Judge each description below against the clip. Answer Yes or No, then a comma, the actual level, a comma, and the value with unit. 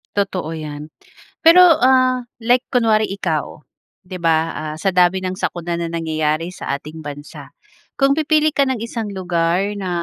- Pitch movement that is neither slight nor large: No, wide, 6.3 semitones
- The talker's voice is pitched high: No, medium, 180 Hz